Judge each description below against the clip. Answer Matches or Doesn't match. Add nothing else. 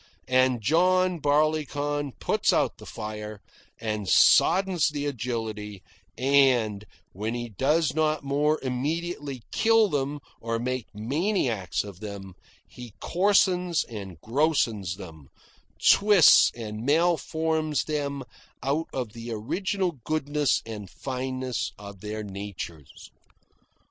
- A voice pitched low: Matches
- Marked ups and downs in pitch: Matches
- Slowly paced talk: Matches